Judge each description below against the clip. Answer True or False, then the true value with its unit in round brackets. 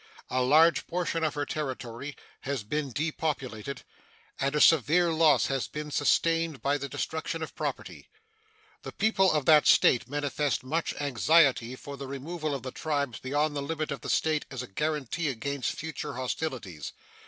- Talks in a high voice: False (145 Hz)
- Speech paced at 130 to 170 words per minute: True (165 wpm)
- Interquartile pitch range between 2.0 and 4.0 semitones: True (3.0 semitones)